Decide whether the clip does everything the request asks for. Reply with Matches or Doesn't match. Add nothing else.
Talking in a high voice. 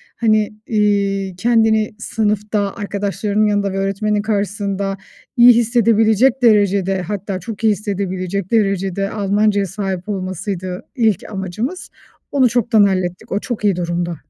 Matches